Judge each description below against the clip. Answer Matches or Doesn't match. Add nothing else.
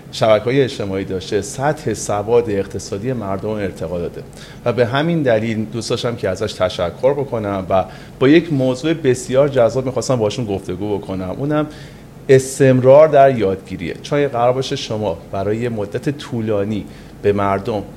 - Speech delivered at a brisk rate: Doesn't match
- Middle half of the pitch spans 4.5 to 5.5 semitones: Matches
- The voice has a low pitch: Matches